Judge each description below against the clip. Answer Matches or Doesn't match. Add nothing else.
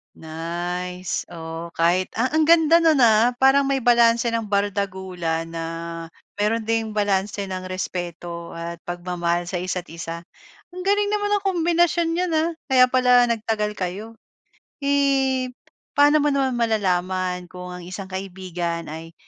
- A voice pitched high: Matches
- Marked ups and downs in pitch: Matches